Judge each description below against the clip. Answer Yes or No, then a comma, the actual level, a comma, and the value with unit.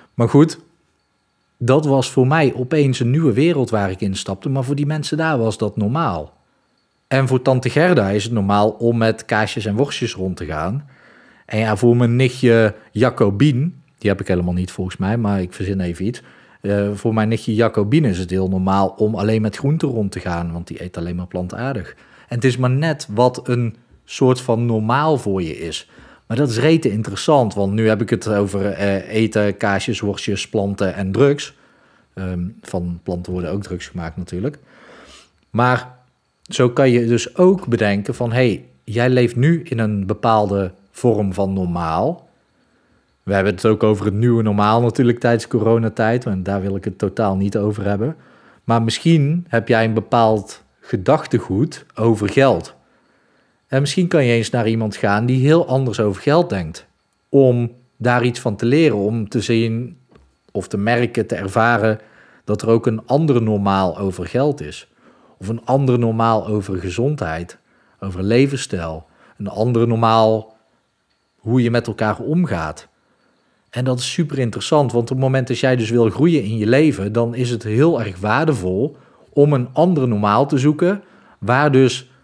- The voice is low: Yes, low, 115 Hz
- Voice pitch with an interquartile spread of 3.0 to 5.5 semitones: Yes, average, 4.2 semitones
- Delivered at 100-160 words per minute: No, average, 180 wpm